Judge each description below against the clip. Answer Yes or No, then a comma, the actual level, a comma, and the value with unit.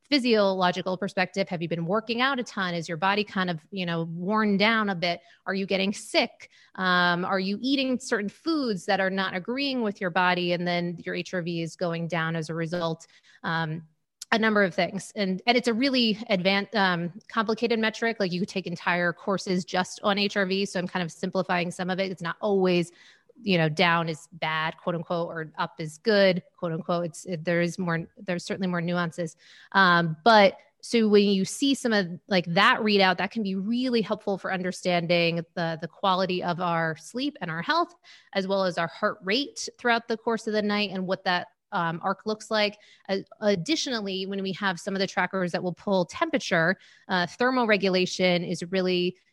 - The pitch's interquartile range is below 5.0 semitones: Yes, average, 3.2 semitones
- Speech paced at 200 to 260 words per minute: Yes, fast, 205 wpm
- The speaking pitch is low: No, high, 190 Hz